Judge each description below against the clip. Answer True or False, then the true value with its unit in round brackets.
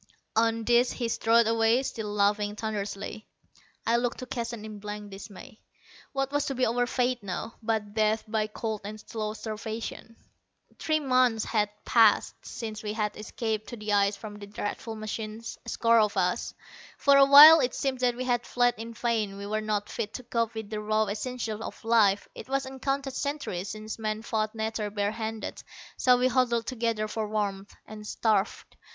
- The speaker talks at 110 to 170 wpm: False (185 wpm)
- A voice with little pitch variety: True (2.2 semitones)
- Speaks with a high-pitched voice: True (220 Hz)